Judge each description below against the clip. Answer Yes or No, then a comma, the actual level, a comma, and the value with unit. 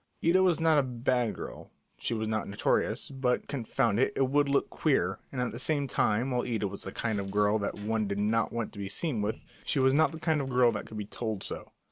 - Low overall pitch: Yes, low, 120 Hz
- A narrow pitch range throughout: No, average, 4.5 semitones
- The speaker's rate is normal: No, fast, 250 wpm